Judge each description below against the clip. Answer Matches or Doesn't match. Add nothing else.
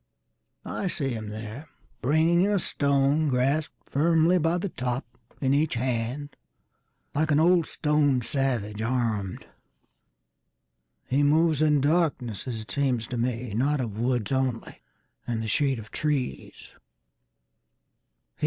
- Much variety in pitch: Doesn't match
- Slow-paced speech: Matches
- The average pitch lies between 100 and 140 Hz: Matches